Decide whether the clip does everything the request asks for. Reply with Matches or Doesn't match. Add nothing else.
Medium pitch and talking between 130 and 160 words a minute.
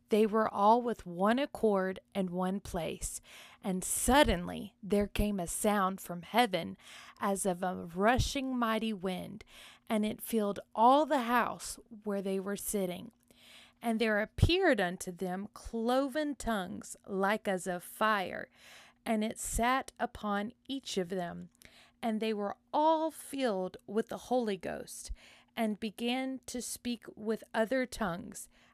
Doesn't match